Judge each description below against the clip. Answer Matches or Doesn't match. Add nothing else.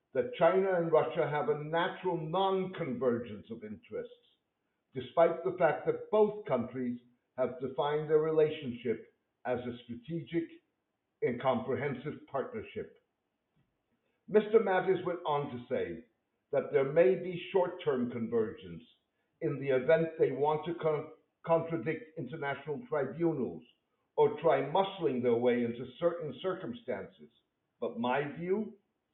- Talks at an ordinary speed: Doesn't match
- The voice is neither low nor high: Matches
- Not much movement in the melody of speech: Doesn't match